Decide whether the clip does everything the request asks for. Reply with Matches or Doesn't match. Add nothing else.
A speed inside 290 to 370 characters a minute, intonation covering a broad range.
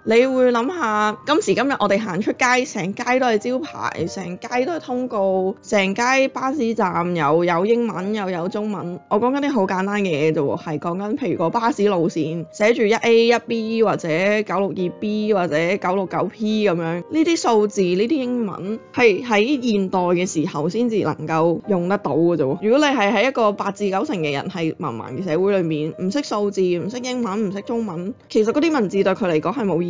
Doesn't match